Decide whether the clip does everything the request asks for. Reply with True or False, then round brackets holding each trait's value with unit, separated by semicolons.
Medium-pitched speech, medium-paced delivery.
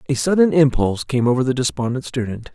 False (130 Hz; 190 wpm)